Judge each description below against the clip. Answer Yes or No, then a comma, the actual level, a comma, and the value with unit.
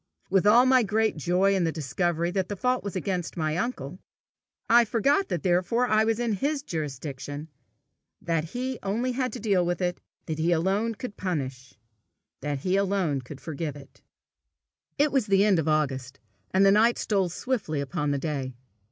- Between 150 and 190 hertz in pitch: Yes, medium, 185 Hz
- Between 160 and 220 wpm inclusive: Yes, average, 180 wpm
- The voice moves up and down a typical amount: No, wide, 6.0 semitones